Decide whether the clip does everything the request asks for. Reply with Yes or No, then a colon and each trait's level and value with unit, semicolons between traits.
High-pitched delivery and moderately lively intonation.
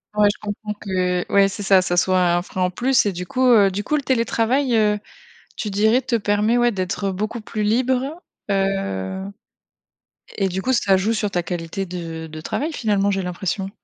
Yes: high, 200 Hz; average, 3.5 semitones